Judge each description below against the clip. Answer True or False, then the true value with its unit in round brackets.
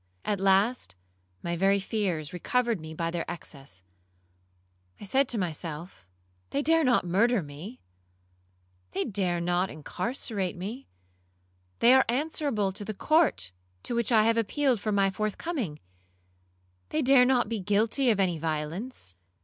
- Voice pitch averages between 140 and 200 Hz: True (190 Hz)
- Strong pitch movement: True (8.6 semitones)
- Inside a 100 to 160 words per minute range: True (135 wpm)